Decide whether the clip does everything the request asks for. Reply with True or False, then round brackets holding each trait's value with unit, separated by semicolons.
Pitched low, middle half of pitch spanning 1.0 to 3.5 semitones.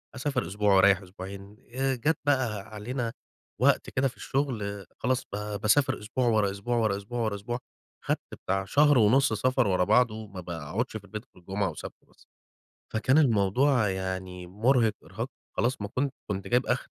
False (105 Hz; 4.2 semitones)